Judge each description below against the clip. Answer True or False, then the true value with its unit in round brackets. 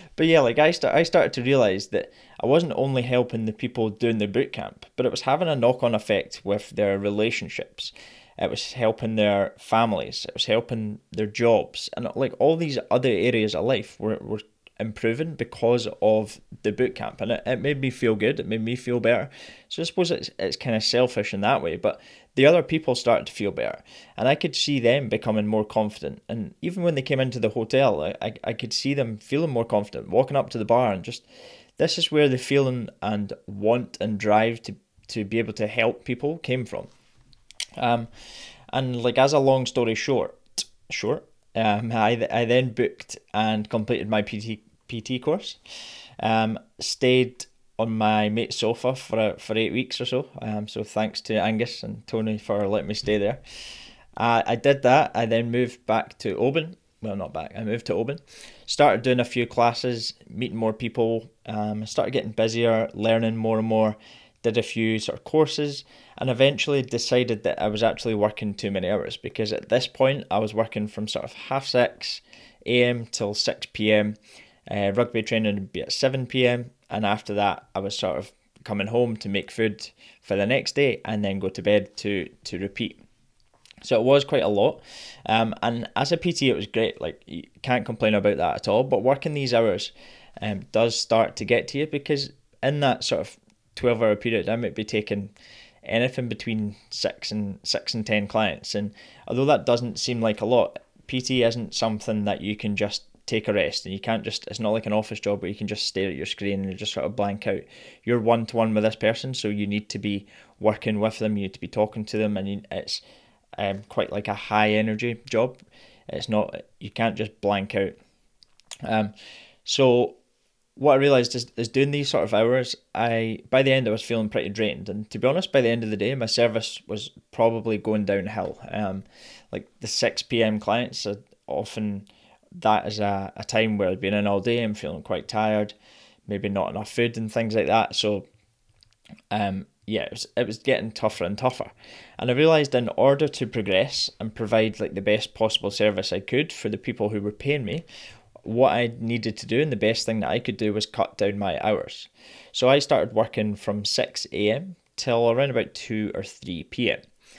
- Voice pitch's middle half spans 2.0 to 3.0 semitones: True (2.7 semitones)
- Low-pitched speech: True (110 Hz)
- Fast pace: True (210 wpm)